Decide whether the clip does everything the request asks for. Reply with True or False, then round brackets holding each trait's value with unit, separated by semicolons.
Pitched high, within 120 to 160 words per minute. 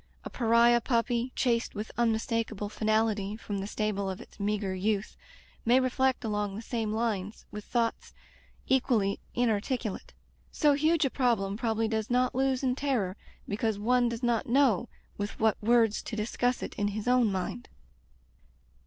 True (225 Hz; 155 wpm)